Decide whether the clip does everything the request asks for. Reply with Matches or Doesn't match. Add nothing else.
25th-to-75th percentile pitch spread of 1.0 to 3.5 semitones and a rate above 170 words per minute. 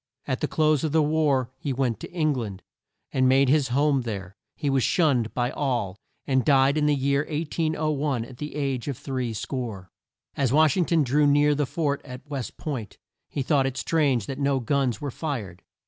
Matches